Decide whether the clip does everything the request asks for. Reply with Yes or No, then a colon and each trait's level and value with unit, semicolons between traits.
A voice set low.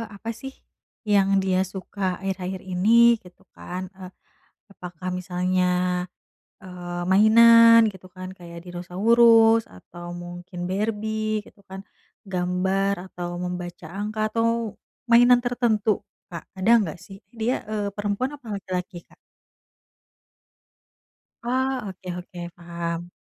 No: high, 190 Hz